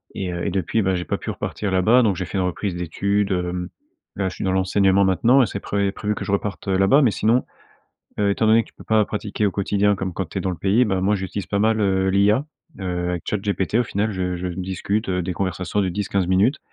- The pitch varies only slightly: Yes, narrow, 2.0 semitones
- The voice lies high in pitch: No, very low, 95 Hz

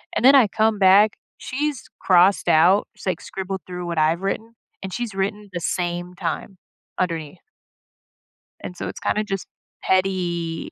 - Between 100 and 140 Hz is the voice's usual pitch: No, high, 190 Hz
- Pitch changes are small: No, average, 3.0 semitones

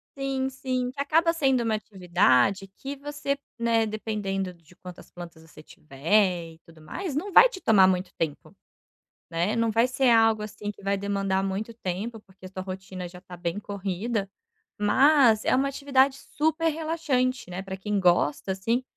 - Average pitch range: No, wide, 5.9 semitones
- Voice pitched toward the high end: Yes, high, 210 Hz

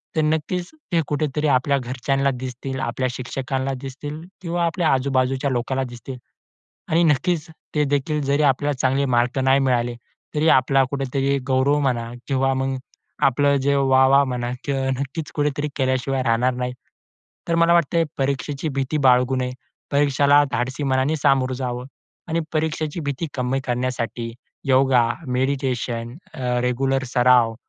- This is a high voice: No, low, 135 Hz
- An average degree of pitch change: No, narrow, 2.2 semitones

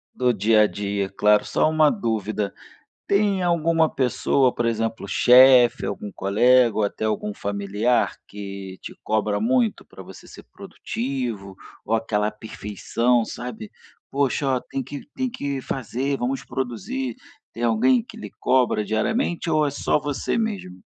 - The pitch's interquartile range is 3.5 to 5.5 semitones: Yes, average, 4.5 semitones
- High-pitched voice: No, low, 120 Hz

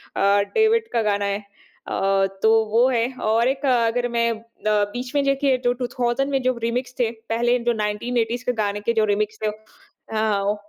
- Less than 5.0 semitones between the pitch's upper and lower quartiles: Yes, average, 2.9 semitones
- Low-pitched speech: No, high, 235 Hz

